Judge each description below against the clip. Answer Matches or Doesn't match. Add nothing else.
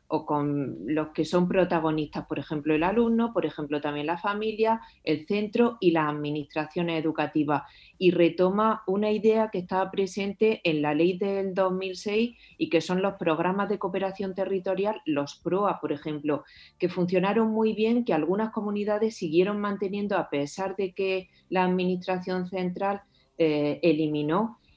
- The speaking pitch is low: Doesn't match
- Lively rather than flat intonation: Doesn't match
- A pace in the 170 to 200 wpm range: Doesn't match